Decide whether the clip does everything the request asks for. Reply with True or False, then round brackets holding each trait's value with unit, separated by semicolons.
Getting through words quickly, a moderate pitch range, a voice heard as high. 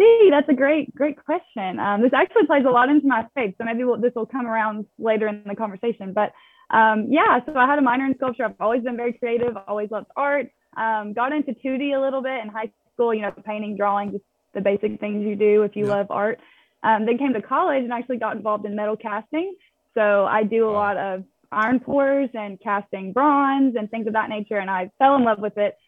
True (235 wpm; 4.1 semitones; 225 Hz)